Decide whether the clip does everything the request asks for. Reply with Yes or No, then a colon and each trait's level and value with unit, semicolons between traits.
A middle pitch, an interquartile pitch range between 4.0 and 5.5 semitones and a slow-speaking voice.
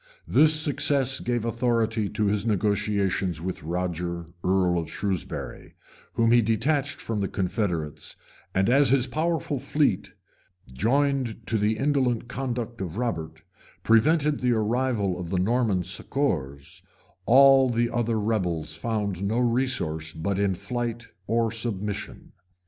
No: low, 110 Hz; average, 5.0 semitones; slow, 130 wpm